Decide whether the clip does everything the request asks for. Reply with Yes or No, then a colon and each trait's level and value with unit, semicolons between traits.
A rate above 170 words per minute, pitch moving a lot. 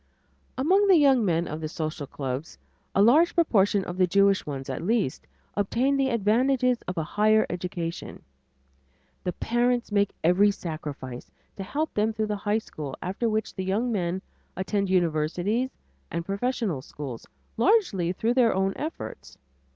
No: average, 155 wpm; wide, 5.7 semitones